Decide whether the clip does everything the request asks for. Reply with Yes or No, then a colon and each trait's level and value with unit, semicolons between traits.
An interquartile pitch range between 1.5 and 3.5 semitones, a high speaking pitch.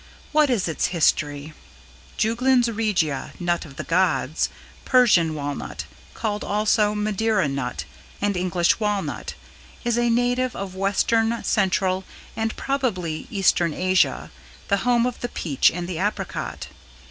No: average, 4.9 semitones; high, 200 Hz